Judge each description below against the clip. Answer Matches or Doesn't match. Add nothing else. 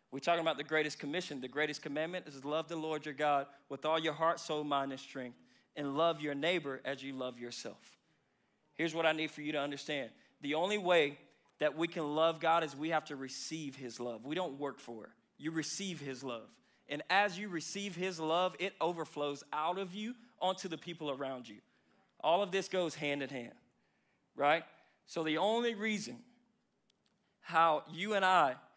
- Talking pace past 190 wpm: Matches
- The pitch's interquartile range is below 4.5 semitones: Matches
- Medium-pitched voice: Matches